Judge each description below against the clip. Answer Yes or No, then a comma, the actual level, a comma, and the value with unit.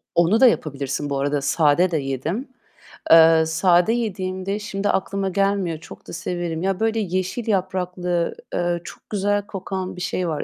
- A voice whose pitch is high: No, medium, 180 Hz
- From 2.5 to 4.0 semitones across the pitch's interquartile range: Yes, average, 3.2 semitones